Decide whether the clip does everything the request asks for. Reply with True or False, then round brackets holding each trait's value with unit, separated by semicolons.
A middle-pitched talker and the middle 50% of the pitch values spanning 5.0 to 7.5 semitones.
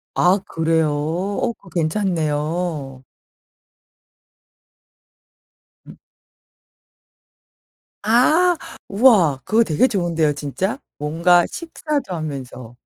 True (170 Hz; 5.4 semitones)